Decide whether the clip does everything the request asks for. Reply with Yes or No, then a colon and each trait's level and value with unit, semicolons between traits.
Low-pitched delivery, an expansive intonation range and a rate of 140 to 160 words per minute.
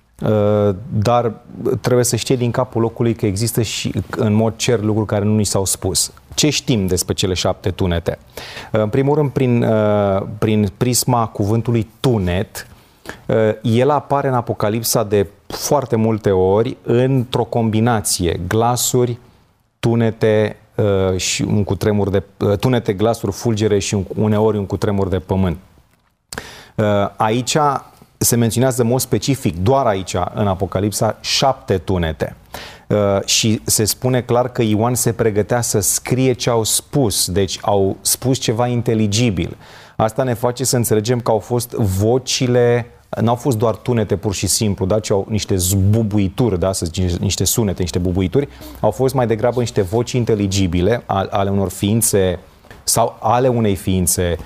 No: low, 110 Hz; average, 3.4 semitones; average, 150 wpm